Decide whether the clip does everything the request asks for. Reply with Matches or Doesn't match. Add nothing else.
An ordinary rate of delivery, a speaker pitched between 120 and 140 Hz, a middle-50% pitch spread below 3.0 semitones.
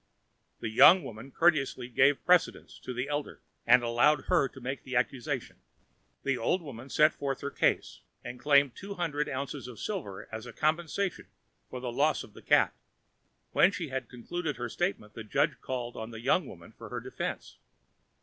Doesn't match